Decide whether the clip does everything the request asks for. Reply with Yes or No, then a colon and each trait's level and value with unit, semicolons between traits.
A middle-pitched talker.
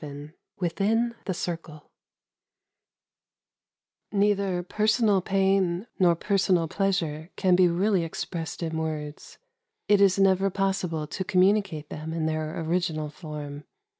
Yes: medium, 180 Hz